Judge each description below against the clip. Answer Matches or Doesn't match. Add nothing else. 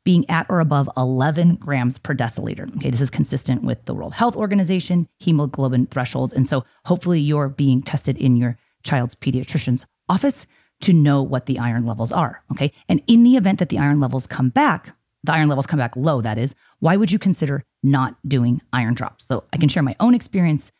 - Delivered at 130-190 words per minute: Doesn't match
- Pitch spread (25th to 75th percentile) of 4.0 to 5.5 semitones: Matches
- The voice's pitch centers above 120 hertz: Matches